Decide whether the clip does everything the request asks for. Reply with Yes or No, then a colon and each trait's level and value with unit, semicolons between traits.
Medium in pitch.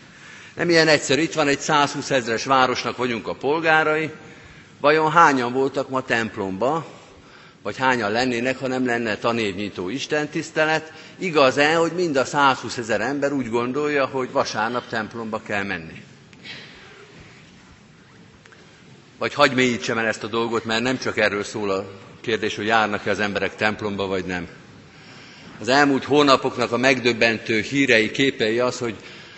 No: low, 125 Hz